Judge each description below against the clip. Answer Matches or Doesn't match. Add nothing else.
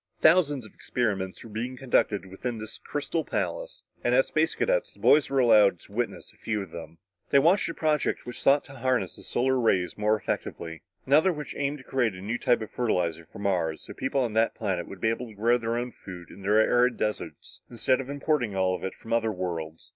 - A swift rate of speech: Matches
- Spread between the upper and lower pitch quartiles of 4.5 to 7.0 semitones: Matches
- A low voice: Matches